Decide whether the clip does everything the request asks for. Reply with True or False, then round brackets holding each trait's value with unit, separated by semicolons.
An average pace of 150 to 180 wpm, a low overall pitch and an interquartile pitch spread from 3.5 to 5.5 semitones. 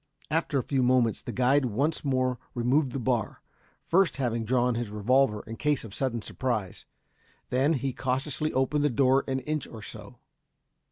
False (170 wpm; 130 Hz; 2.5 semitones)